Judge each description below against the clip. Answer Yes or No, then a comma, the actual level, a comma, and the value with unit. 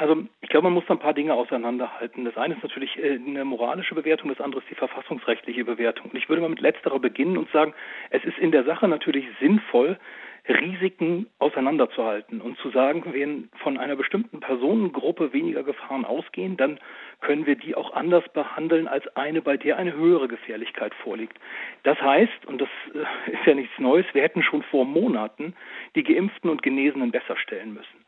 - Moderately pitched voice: Yes, medium, 160 Hz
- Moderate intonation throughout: No, wide, 6.3 semitones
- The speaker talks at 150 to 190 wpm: Yes, average, 185 wpm